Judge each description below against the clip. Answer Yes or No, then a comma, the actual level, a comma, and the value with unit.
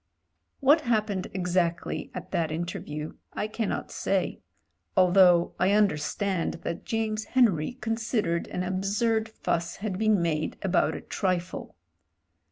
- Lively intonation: No, average, 4.1 semitones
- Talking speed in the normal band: No, slow, 125 wpm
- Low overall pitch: No, high, 190 Hz